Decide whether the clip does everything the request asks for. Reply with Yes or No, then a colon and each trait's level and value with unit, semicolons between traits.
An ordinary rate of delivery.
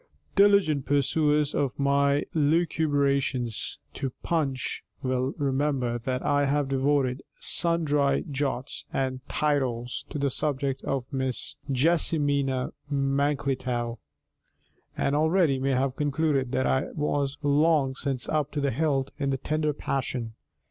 No: slow, 125 wpm